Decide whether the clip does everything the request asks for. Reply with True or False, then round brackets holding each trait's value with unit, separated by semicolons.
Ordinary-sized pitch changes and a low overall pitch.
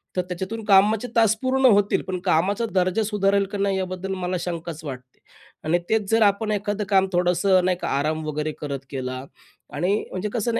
False (3.0 semitones; 190 Hz)